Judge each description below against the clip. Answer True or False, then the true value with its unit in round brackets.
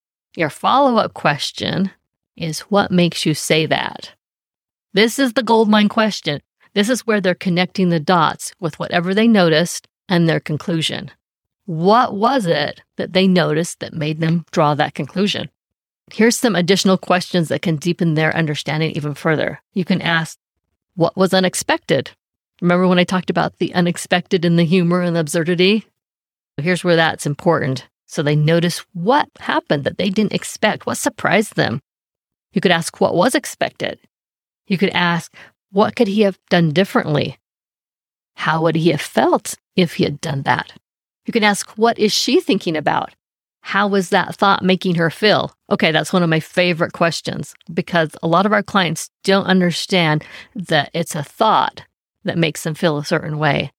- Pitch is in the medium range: True (175 Hz)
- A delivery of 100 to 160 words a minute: False (170 wpm)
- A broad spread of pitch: False (3.3 semitones)